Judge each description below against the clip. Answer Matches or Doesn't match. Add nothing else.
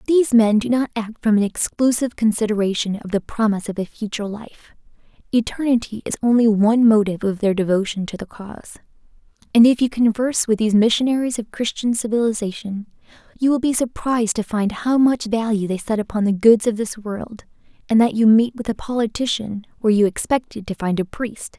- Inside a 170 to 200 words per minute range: Matches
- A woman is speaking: Matches